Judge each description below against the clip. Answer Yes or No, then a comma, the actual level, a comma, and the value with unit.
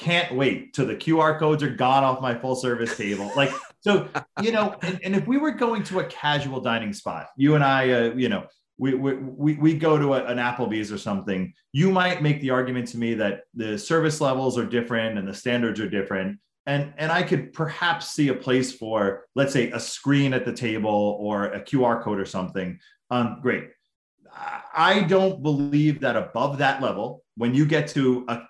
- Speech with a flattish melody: No, average, 4.9 semitones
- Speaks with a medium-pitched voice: No, low, 130 Hz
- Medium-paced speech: No, fast, 210 wpm